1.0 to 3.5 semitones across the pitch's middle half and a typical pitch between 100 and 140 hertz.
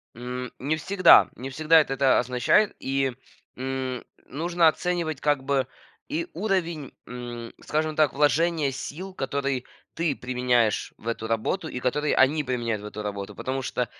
No: average, 4.0 semitones; low, 135 Hz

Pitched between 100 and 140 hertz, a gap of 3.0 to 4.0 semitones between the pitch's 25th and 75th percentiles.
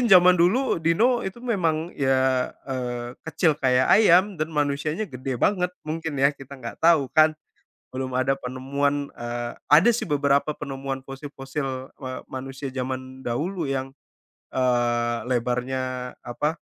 Yes: low, 135 Hz; average, 3.7 semitones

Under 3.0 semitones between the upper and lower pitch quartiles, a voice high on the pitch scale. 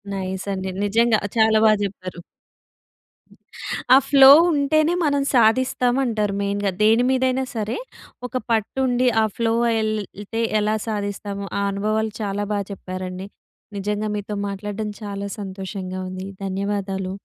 Yes: narrow, 2.4 semitones; high, 205 Hz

